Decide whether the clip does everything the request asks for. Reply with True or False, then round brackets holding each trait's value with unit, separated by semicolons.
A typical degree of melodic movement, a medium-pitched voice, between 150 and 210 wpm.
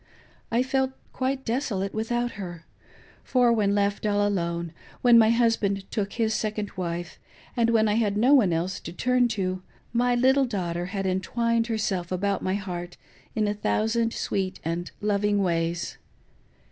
False (3.9 semitones; 205 Hz; 160 wpm)